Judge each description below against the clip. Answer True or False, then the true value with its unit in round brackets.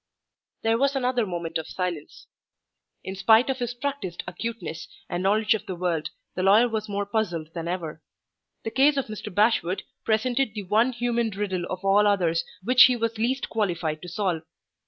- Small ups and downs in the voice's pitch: False (4.6 semitones)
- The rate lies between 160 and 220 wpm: True (180 wpm)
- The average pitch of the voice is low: False (210 Hz)